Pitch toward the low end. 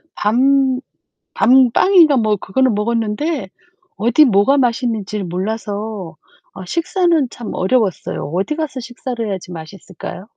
No: high, 230 Hz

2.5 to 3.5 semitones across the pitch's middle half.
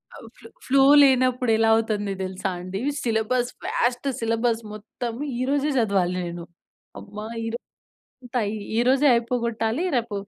Yes: average, 2.9 semitones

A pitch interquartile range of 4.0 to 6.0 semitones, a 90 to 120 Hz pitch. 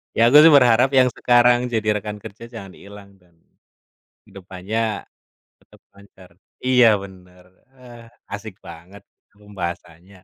Yes: average, 4.5 semitones; low, 100 Hz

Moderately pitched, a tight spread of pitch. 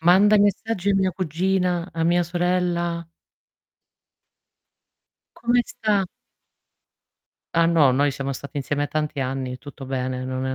No: medium, 170 Hz; average, 4.9 semitones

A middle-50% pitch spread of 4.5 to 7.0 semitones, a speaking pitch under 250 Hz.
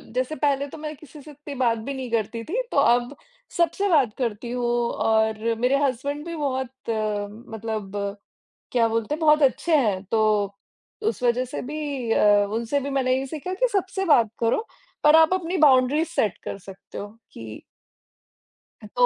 No: average, 5.0 semitones; very high, 255 Hz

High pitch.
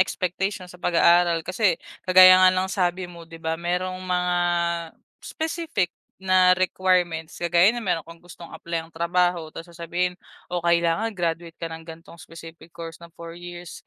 No: medium, 175 Hz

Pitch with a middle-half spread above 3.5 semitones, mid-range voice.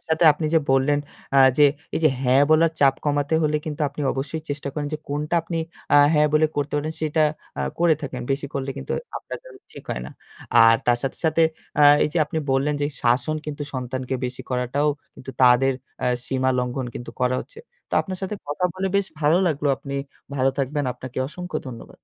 No: average, 3.0 semitones; medium, 145 Hz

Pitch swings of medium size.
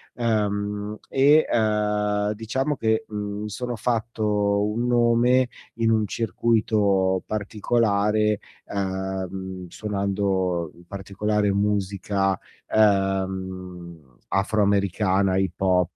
No: narrow, 2.1 semitones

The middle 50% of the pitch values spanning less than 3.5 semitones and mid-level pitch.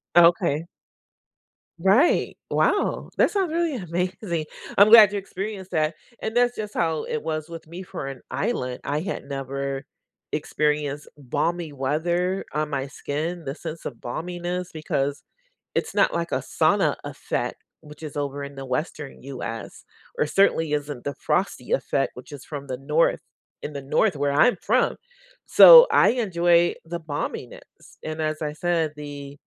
No: average, 3.8 semitones; medium, 155 Hz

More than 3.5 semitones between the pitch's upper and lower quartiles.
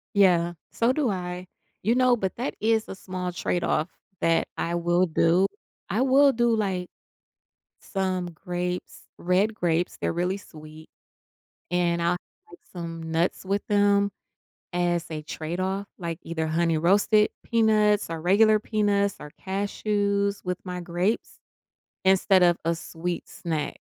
No: average, 3.0 semitones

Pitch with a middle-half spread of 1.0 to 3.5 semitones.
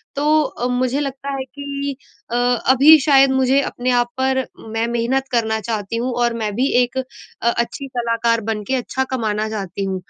Yes: average, 2.7 semitones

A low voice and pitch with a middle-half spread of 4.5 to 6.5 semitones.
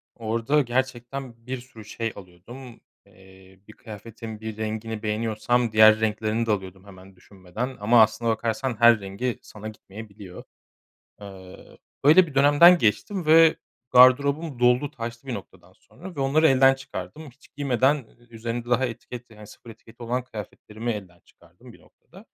No: low, 115 Hz; average, 3.5 semitones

